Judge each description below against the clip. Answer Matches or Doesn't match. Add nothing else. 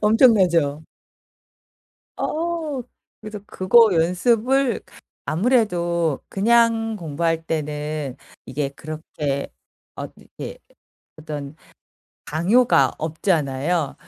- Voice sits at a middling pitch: Matches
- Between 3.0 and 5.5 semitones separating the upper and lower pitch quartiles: Doesn't match